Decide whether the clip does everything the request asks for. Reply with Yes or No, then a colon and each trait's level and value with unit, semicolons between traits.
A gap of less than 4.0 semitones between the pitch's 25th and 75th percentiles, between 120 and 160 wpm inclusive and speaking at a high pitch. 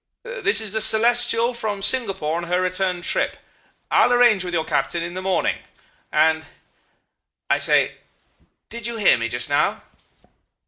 No: average, 5.1 semitones; average, 150 wpm; high, 195 Hz